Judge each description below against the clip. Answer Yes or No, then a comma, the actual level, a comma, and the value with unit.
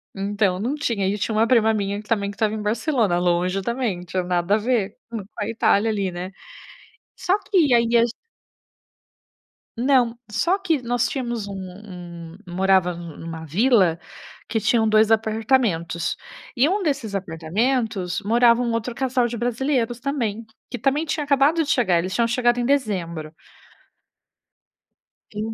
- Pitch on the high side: Yes, high, 225 Hz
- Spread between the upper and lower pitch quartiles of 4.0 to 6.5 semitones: Yes, average, 4.4 semitones